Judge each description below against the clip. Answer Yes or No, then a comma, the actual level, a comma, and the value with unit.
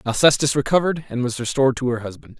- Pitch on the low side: Yes, low, 130 Hz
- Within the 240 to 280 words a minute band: No, average, 200 wpm